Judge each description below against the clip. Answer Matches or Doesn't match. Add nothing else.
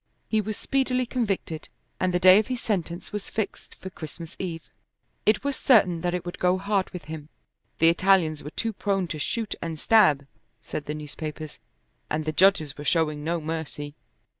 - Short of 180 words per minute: Doesn't match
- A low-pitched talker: Doesn't match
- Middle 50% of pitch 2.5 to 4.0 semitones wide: Doesn't match